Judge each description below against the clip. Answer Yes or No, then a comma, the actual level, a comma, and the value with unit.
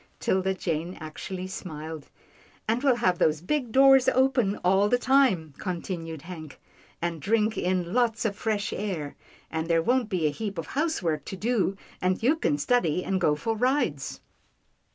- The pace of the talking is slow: No, average, 175 wpm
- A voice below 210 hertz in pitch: Yes, high, 190 Hz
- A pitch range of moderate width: No, wide, 6.4 semitones